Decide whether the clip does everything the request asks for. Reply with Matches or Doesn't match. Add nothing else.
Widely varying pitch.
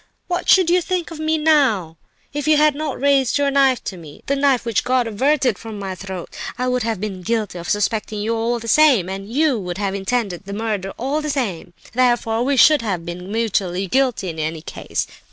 Matches